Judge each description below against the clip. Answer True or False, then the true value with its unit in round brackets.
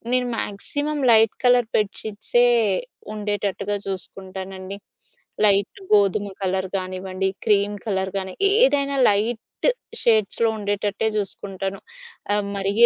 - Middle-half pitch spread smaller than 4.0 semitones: True (2.4 semitones)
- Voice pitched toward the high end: True (205 Hz)